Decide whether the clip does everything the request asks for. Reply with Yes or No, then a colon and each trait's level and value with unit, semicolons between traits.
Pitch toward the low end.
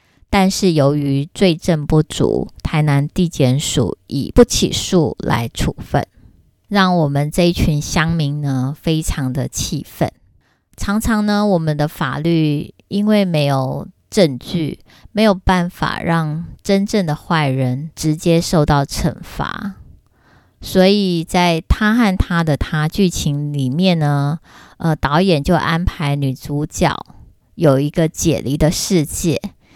No: medium, 160 Hz